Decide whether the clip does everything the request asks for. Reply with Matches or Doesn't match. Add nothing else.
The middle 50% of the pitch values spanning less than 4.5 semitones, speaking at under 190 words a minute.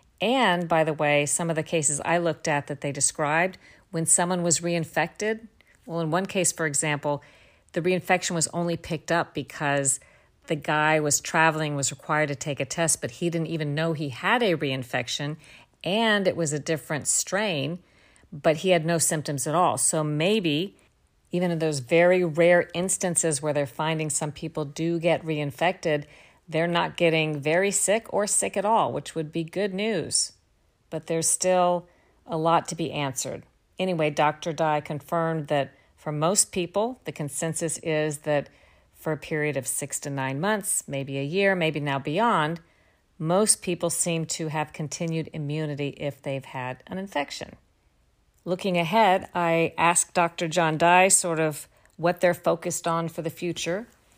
Matches